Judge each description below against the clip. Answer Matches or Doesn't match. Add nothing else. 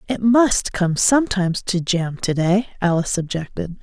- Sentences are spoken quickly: Doesn't match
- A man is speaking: Doesn't match